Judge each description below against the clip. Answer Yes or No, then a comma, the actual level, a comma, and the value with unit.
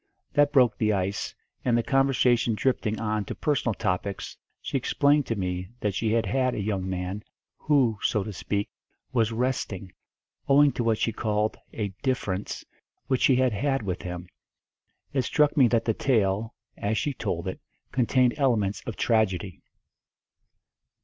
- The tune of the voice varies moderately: Yes, average, 4.3 semitones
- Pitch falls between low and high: No, low, 110 Hz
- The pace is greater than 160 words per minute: No, average, 155 wpm